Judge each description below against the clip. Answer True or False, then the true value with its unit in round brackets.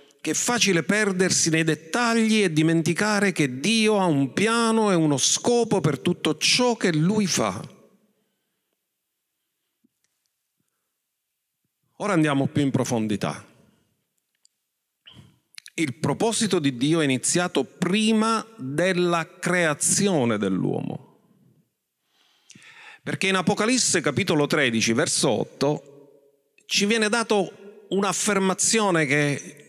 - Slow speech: True (95 wpm)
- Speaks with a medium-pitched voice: True (175 Hz)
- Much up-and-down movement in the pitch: True (5.9 semitones)